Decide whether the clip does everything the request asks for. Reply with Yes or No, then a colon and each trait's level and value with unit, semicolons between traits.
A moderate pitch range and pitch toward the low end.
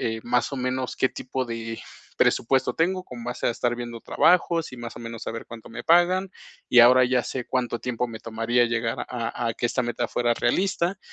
No: narrow, 1.9 semitones; low, 120 Hz